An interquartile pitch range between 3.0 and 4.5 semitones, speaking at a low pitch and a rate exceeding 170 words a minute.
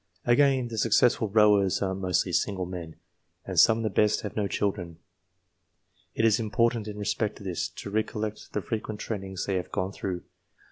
No: narrow, 2.5 semitones; low, 105 Hz; average, 180 wpm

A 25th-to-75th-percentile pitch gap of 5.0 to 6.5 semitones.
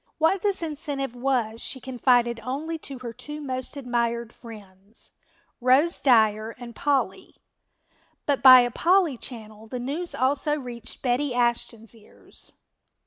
No: average, 3.5 semitones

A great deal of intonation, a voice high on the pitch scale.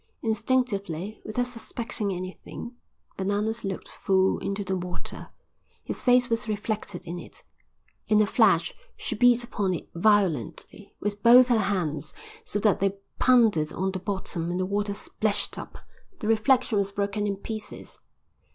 No: average, 2.8 semitones; high, 205 Hz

